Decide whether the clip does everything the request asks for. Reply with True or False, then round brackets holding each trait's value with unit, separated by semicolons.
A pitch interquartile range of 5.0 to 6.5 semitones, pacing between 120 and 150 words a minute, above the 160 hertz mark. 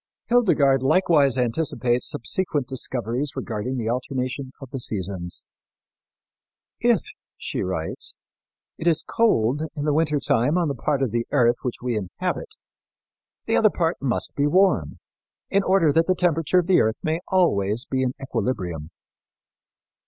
False (5.4 semitones; 145 wpm; 135 Hz)